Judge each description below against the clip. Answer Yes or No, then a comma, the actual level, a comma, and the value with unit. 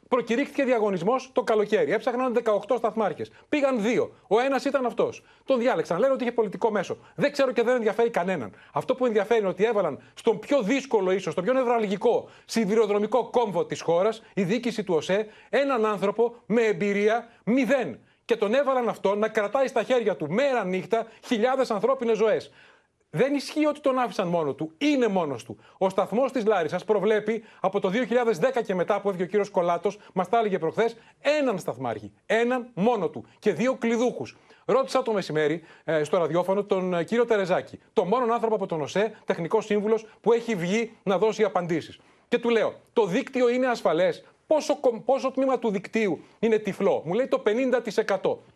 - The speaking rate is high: Yes, fast, 175 wpm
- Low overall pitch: No, high, 225 Hz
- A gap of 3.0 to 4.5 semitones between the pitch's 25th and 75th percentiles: Yes, average, 3.9 semitones